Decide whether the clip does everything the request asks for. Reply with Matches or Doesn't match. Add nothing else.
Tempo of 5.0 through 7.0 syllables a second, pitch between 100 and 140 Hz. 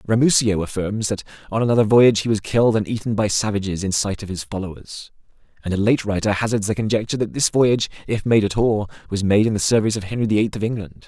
Matches